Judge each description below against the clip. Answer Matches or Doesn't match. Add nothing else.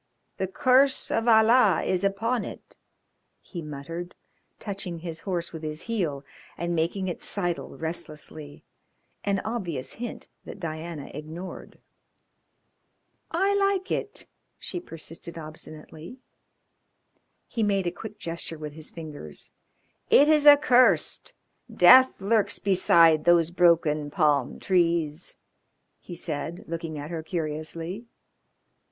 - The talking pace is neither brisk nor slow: Doesn't match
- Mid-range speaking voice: Matches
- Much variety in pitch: Doesn't match